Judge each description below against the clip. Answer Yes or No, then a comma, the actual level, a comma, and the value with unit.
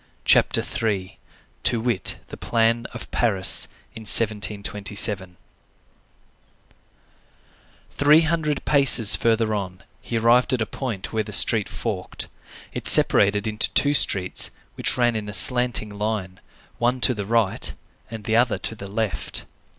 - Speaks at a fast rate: No, slow, 135 wpm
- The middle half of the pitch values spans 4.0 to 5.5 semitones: No, average, 2.8 semitones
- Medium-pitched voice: No, low, 110 Hz